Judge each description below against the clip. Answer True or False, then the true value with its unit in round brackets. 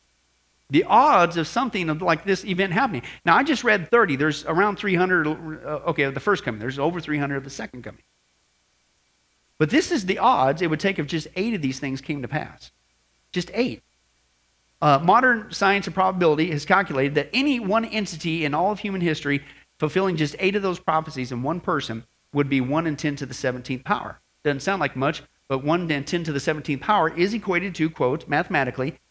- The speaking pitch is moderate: True (155 Hz)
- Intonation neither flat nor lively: False (5.9 semitones)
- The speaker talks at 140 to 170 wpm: False (200 wpm)